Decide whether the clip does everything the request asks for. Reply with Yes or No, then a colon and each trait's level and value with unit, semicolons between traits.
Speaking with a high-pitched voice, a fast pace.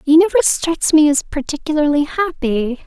No: very high, 300 Hz; average, 145 wpm